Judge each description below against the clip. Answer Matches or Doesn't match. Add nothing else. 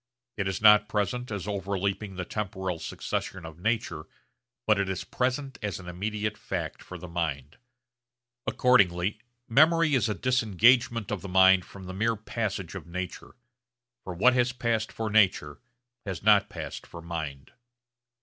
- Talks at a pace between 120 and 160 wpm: Matches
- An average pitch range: Matches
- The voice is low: Matches